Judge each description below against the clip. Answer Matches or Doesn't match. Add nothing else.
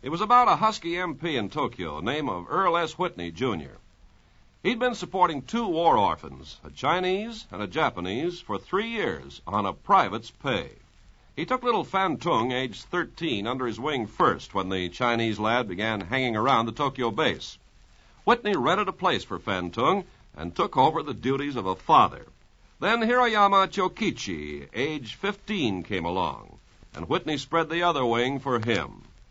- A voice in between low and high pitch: Matches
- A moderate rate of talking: Matches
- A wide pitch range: Matches